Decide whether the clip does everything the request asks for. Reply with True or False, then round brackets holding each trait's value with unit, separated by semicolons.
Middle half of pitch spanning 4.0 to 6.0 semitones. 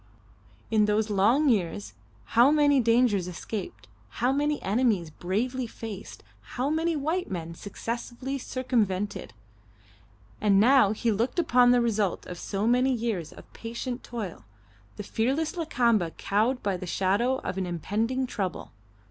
True (4.6 semitones)